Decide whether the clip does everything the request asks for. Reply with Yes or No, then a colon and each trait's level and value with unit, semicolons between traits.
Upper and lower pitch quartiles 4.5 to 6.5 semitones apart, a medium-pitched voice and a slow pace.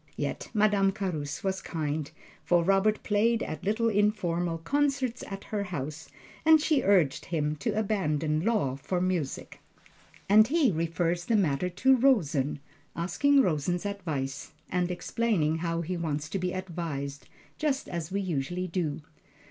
No: average, 4.9 semitones; medium, 180 Hz; average, 145 wpm